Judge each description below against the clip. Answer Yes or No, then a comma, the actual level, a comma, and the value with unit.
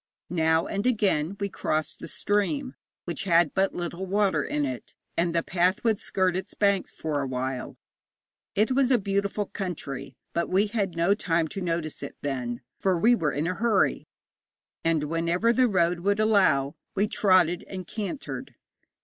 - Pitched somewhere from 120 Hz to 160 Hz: No, medium, 180 Hz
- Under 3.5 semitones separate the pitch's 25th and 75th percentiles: No, average, 3.9 semitones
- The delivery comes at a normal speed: Yes, average, 165 wpm